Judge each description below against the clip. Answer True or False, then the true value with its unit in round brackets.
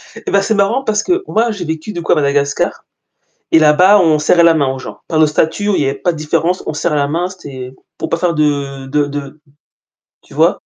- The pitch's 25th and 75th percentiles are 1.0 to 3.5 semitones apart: False (4.1 semitones)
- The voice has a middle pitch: True (160 Hz)